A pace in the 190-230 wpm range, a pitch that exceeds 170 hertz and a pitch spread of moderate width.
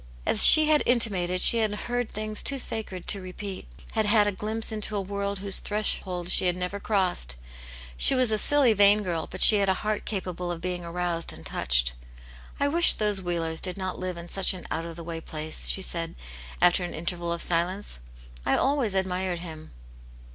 Yes: average, 200 wpm; high, 190 Hz; average, 3.3 semitones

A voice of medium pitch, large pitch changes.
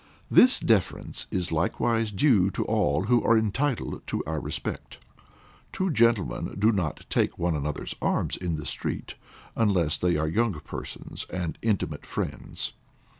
No: very low, 95 Hz; wide, 5.9 semitones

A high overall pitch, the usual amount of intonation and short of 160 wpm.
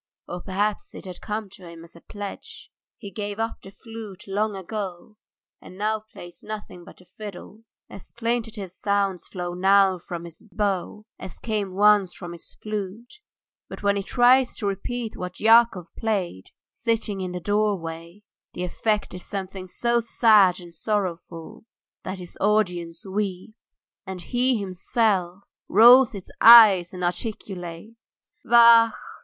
Yes: high, 200 Hz; average, 3.2 semitones; average, 150 wpm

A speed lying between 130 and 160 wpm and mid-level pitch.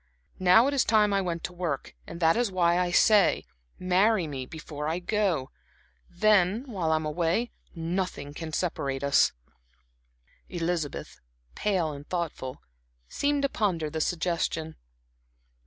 Yes: average, 140 wpm; medium, 175 Hz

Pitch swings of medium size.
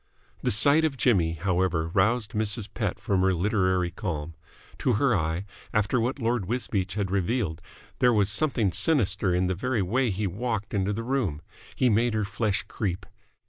Yes: average, 4.0 semitones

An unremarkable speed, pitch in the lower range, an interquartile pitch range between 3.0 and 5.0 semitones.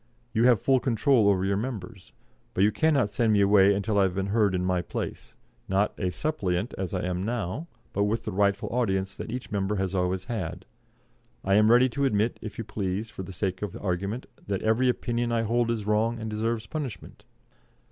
No: fast, 210 wpm; low, 105 Hz; average, 3.4 semitones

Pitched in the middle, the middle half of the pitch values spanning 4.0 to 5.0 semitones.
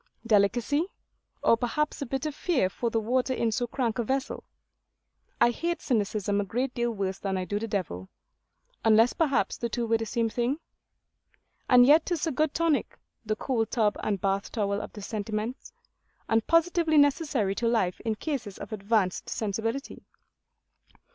No: high, 230 Hz; average, 4.3 semitones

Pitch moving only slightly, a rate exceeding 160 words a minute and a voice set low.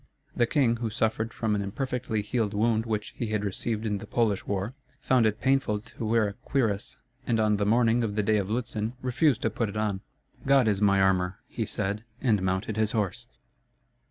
Yes: narrow, 2.3 semitones; fast, 205 wpm; low, 110 Hz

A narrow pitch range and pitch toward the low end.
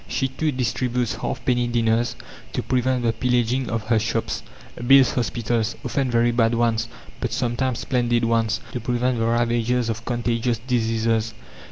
Yes: narrow, 1.5 semitones; low, 120 Hz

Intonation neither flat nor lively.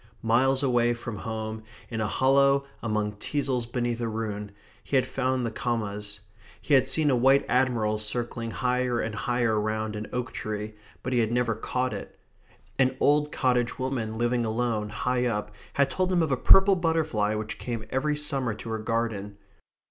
Yes: average, 3.1 semitones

